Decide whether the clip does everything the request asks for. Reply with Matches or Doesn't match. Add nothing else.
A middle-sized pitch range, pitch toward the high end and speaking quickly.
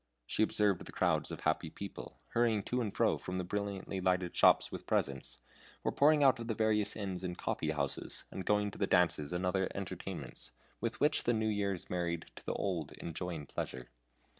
Doesn't match